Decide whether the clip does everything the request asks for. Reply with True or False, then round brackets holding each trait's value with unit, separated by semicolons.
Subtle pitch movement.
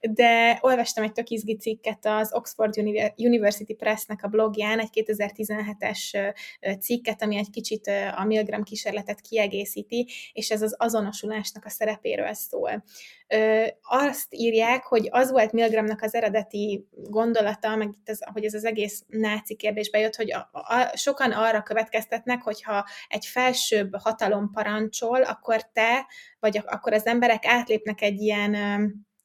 True (1.4 semitones)